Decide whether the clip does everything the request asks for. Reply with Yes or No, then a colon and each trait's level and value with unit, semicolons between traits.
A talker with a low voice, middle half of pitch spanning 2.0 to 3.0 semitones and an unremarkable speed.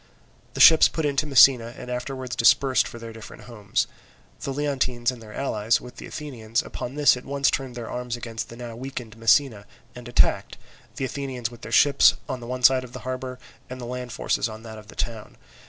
No: low, 125 Hz; narrow, 2.4 semitones; fast, 210 wpm